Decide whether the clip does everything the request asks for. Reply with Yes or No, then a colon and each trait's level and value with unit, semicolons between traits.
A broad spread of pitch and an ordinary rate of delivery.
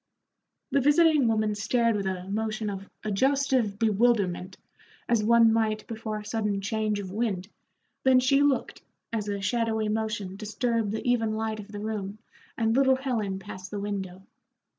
No: narrow, 2.4 semitones; average, 160 wpm